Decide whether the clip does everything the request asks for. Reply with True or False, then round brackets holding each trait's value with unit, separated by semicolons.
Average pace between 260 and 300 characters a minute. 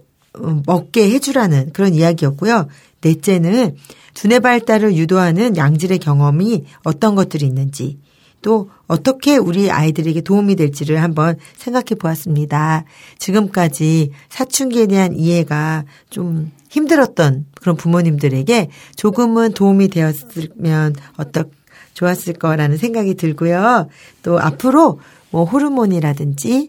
True (290 characters per minute)